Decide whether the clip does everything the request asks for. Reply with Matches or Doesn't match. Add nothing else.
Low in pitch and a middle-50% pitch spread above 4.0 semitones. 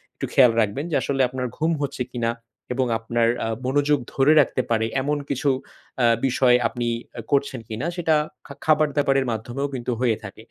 Doesn't match